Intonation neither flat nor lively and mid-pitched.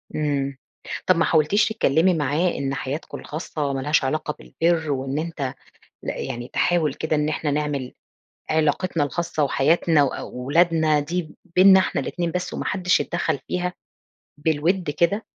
Yes: average, 3.2 semitones; medium, 155 Hz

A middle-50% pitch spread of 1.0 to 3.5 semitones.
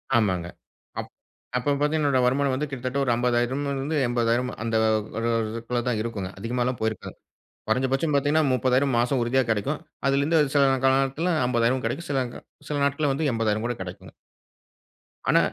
Yes: average, 3.1 semitones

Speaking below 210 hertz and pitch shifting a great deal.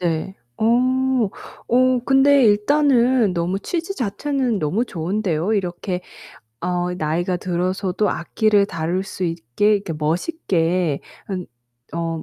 No: medium, 185 Hz; average, 4.9 semitones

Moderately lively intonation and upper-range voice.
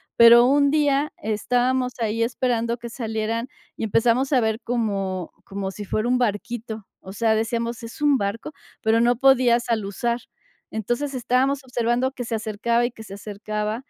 No: narrow, 2.3 semitones; high, 235 Hz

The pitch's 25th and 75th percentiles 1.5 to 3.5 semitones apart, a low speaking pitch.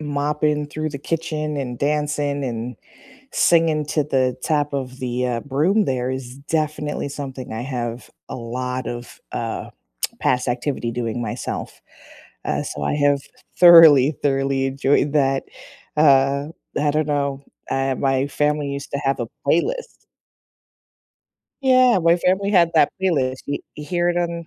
No: average, 2.7 semitones; medium, 145 Hz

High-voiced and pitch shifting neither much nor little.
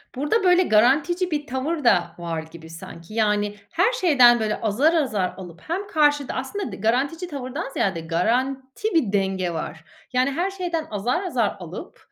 No: very high, 255 Hz; wide, 8.3 semitones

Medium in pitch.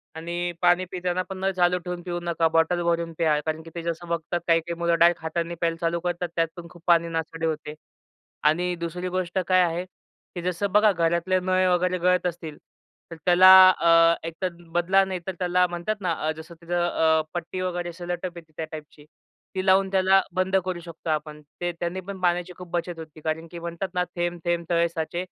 Yes: medium, 175 Hz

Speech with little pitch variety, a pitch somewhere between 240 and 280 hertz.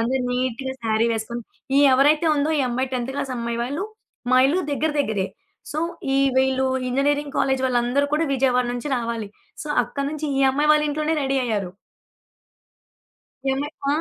No: average, 3.3 semitones; very high, 265 Hz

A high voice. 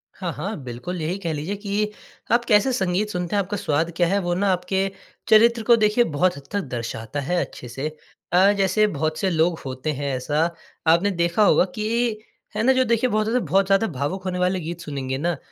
No: medium, 180 Hz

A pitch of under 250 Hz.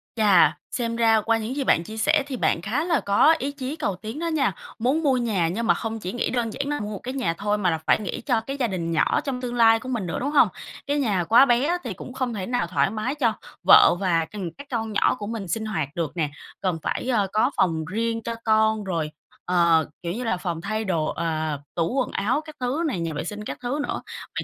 Yes: high, 220 Hz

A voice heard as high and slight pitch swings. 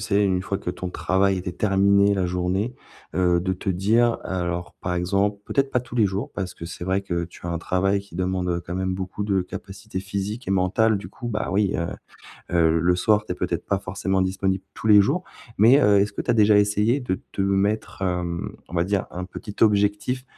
No: very low, 95 Hz; narrow, 2.2 semitones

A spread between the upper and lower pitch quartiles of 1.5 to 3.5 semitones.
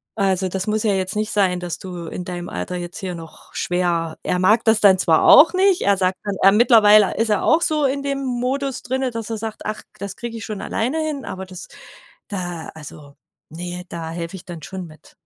No: average, 4.4 semitones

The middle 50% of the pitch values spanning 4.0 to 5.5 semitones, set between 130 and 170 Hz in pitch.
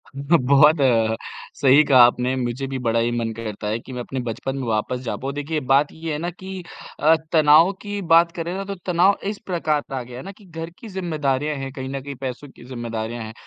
Yes: average, 4.8 semitones; medium, 140 Hz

